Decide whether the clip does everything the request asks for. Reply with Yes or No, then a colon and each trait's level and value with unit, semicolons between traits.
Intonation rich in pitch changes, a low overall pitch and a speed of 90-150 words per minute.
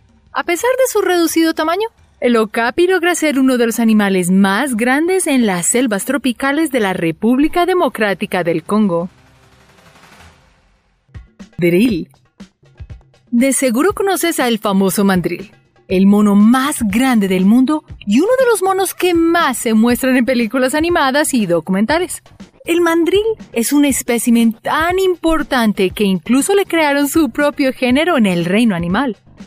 No: wide, 7.7 semitones; very high, 255 Hz; average, 145 wpm